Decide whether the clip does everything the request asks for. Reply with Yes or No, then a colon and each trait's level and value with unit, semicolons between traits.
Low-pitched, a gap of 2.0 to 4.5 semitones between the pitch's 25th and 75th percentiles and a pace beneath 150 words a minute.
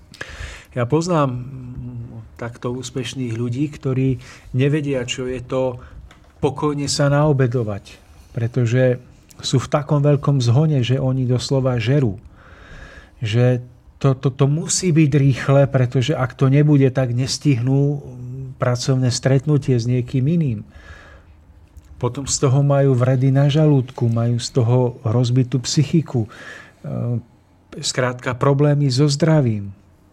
Yes: low, 130 Hz; narrow, 2.5 semitones; slow, 115 wpm